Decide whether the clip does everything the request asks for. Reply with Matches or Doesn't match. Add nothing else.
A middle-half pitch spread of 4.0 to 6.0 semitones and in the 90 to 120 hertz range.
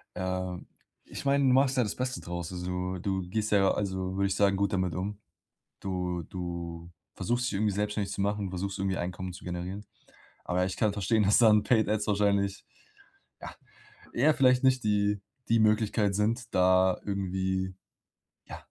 Doesn't match